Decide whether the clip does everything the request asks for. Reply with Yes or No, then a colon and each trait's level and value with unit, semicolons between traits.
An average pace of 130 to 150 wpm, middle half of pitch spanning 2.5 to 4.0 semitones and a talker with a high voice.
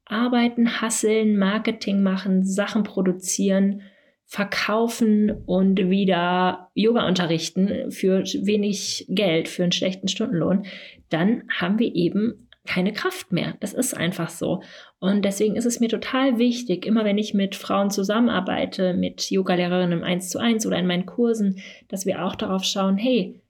Yes: average, 145 wpm; average, 3.0 semitones; high, 200 Hz